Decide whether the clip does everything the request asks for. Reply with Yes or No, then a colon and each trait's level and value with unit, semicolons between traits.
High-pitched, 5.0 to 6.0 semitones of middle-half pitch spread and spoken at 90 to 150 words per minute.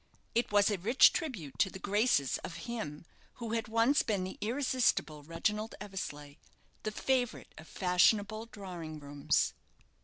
Yes: high, 205 Hz; wide, 5.5 semitones; average, 145 wpm